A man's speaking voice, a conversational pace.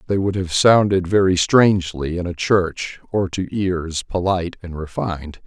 Yes: male; average, 165 wpm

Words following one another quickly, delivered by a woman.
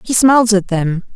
Yes: fast, 210 wpm; female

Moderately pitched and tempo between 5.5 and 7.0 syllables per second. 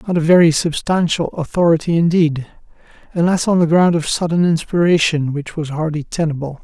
Yes: medium, 165 Hz; 5.6 syllables/s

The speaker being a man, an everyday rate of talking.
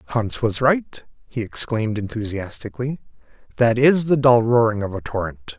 Yes: male; average, 150 wpm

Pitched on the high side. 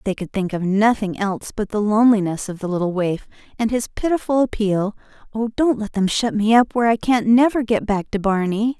Yes: high, 215 Hz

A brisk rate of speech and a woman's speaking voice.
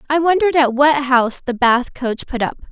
Yes: fast, 220 wpm; female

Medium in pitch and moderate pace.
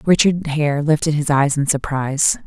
Yes: medium, 150 Hz; average, 170 wpm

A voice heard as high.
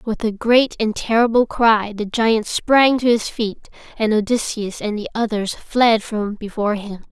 Yes: high, 220 Hz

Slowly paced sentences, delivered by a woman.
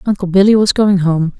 No: fast, 215 wpm; female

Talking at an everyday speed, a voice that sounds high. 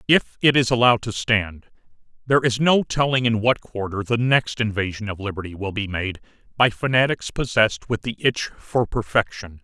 No: average, 180 wpm; low, 115 Hz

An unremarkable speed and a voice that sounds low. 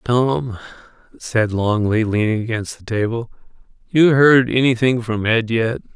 No: slow, 130 wpm; low, 115 Hz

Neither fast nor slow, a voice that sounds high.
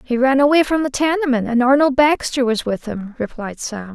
No: fast, 215 wpm; very high, 255 Hz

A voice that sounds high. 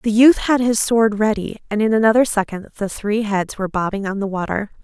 Yes: high, 210 Hz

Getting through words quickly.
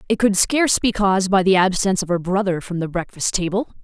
Yes: fast, 235 wpm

